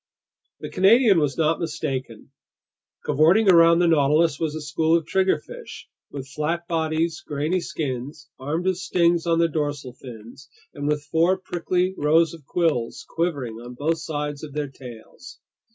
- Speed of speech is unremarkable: Yes, average, 150 wpm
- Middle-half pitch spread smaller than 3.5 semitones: Yes, average, 2.8 semitones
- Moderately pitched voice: Yes, medium, 155 Hz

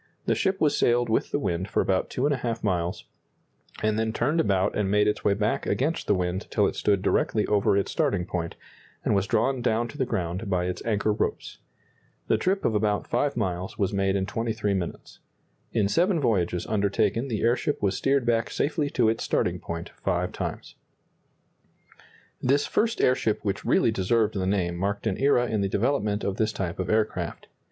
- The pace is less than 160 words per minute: No, average, 190 wpm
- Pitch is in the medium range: No, low, 105 Hz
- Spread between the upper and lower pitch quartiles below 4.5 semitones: Yes, average, 3.6 semitones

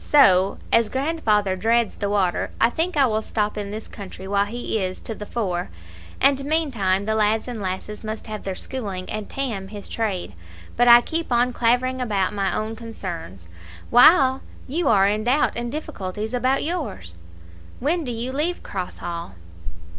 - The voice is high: Yes, high, 220 Hz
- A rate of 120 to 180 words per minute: Yes, average, 175 wpm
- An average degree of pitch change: Yes, average, 4.5 semitones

